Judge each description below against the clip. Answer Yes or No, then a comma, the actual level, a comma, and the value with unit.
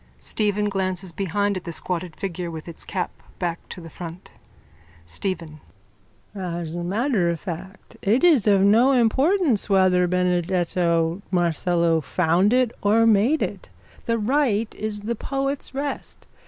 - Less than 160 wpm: Yes, average, 140 wpm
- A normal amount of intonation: Yes, average, 4.3 semitones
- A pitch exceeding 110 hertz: Yes, high, 190 Hz